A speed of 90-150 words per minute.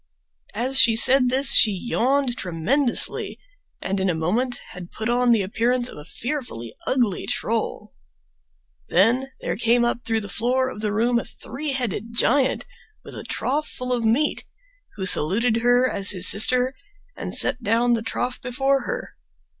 No: average, 165 wpm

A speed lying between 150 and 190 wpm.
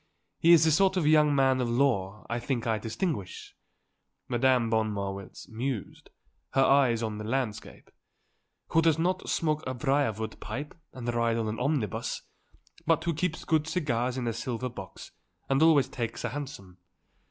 Yes: average, 170 wpm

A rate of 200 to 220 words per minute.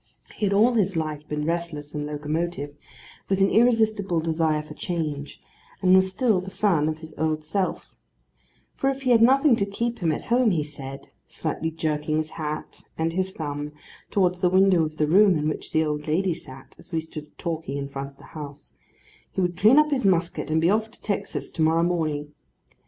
Yes: fast, 205 wpm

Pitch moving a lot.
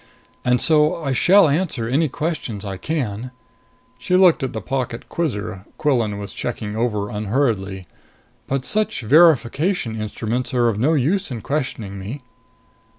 Yes: wide, 6.0 semitones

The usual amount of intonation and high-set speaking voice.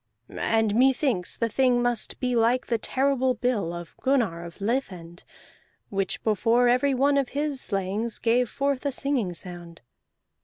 Yes: average, 4.9 semitones; high, 240 Hz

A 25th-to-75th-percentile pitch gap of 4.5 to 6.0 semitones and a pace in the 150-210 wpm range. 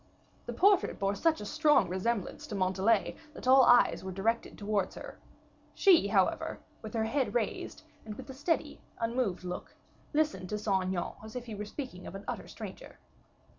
Yes: average, 5.0 semitones; average, 180 wpm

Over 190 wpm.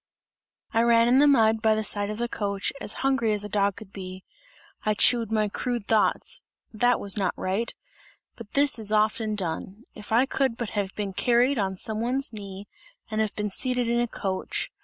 Yes: average, 200 wpm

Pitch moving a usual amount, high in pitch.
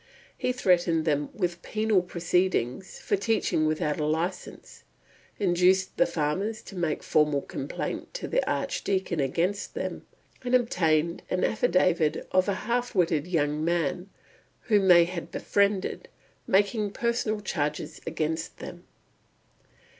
No: average, 4.2 semitones; medium, 180 Hz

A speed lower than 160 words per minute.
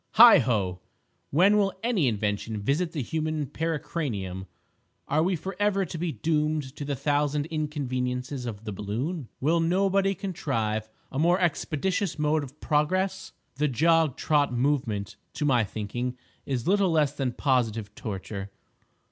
Yes: average, 140 wpm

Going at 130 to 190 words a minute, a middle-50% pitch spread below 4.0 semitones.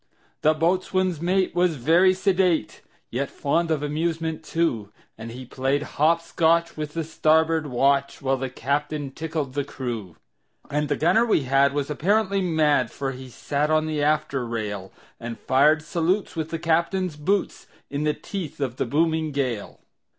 Yes: average, 165 wpm; average, 3.5 semitones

